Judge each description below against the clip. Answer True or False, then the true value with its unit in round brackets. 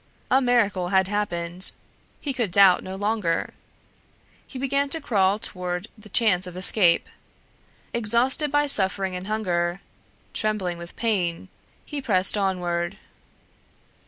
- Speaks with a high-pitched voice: True (195 Hz)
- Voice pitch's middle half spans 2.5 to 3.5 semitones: False (4.3 semitones)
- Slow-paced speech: True (125 wpm)